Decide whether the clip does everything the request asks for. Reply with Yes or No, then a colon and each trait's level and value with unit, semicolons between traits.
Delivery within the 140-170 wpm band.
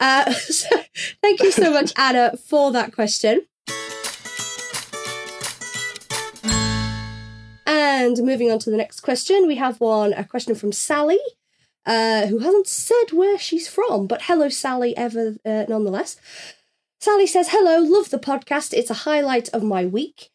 Yes: average, 145 wpm